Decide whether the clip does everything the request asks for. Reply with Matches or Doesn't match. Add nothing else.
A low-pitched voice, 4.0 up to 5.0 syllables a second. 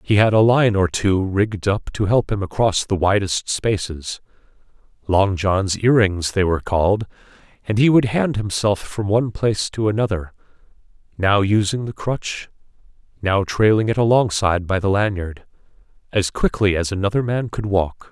Matches